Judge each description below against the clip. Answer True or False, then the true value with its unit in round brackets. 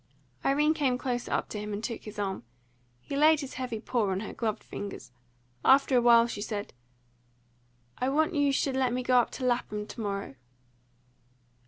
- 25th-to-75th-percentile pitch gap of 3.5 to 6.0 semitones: True (4.2 semitones)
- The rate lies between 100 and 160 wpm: False (185 wpm)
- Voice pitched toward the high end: True (245 Hz)